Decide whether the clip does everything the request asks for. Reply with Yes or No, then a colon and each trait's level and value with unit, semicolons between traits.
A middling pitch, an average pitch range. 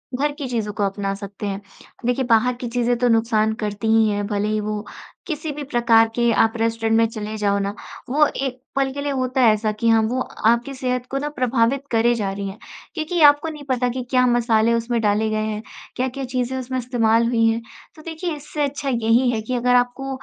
No: high, 235 Hz; average, 3.1 semitones